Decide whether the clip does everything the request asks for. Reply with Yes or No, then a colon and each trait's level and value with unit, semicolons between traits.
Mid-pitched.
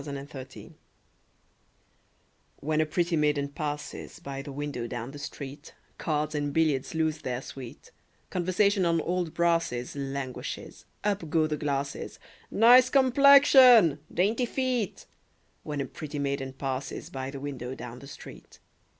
Yes: medium, 150 Hz